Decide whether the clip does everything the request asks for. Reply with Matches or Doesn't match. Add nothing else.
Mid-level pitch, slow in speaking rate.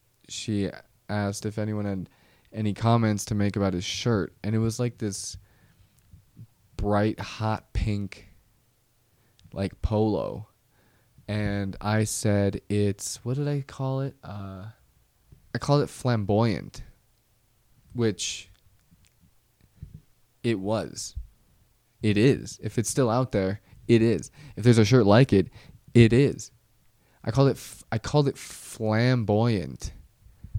Doesn't match